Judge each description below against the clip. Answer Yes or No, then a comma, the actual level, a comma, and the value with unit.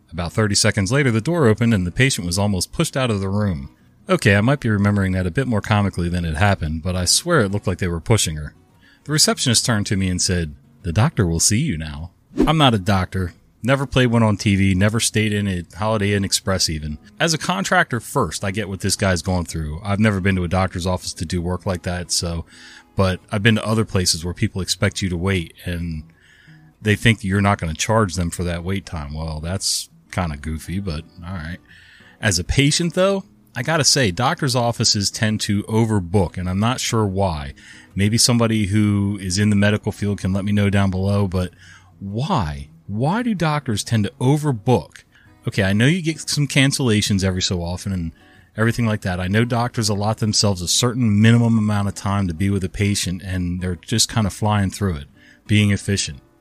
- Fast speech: Yes, fast, 220 wpm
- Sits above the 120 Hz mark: No, low, 100 Hz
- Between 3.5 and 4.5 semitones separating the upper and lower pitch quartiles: Yes, average, 3.9 semitones